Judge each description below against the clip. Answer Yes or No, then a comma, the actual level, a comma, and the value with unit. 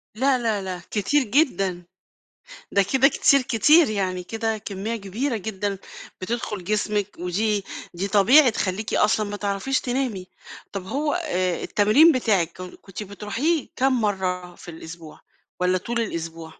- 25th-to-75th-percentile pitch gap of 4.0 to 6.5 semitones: Yes, average, 4.6 semitones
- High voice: Yes, high, 210 Hz